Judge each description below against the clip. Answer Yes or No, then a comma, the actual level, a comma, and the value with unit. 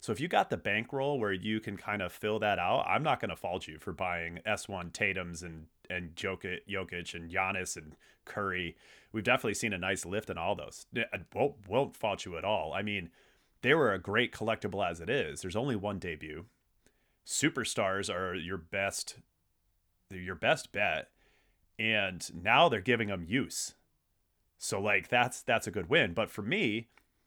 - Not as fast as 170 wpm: No, average, 185 wpm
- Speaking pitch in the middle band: No, very low, 95 Hz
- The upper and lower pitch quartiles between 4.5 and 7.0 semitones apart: No, average, 2.9 semitones